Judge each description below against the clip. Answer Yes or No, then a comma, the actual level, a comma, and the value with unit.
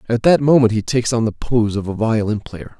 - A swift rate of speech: Yes, fast, 260 wpm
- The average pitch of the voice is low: Yes, low, 115 Hz